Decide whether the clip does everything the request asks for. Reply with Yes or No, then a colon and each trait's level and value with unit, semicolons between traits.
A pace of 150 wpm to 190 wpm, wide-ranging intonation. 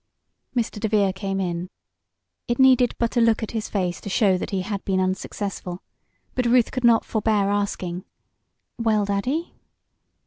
No: average, 160 wpm; average, 3.4 semitones